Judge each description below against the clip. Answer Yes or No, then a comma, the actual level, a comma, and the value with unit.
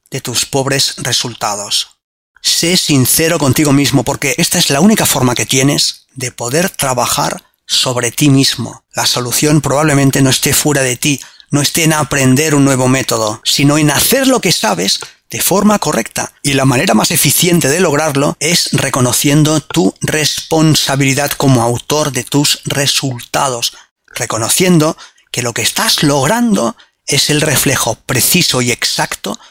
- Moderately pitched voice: Yes, medium, 145 Hz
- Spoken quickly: No, average, 150 wpm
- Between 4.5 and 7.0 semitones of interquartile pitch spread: No, average, 2.9 semitones